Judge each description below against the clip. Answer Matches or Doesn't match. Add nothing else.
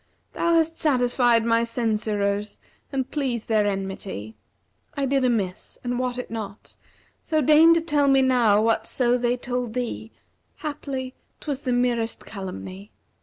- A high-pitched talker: Matches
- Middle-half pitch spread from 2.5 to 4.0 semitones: Matches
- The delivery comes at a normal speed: Matches